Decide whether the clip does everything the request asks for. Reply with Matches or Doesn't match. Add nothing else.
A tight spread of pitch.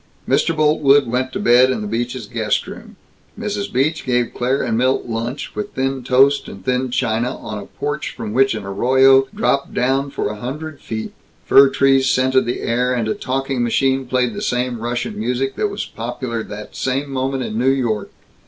Matches